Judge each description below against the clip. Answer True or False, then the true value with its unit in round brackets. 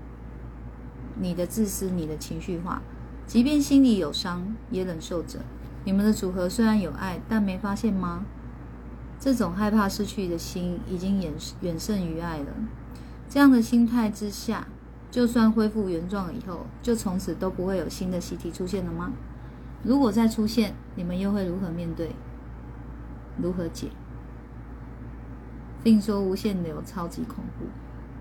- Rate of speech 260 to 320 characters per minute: False (220 characters per minute)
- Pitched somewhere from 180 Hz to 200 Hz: True (190 Hz)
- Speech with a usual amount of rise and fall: True (4.1 semitones)